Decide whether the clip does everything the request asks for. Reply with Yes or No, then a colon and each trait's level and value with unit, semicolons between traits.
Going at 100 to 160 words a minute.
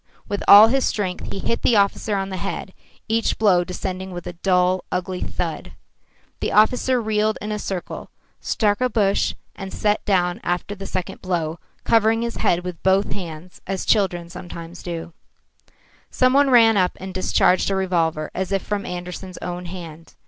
No: average, 170 wpm